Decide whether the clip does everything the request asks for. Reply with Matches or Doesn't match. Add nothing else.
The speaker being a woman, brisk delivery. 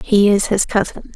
Matches